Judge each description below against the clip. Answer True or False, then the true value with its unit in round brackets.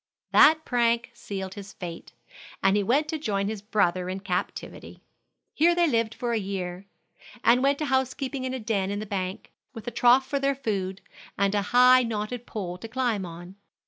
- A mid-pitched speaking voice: False (220 Hz)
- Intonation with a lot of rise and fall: False (4.8 semitones)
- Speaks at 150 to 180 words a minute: False (190 wpm)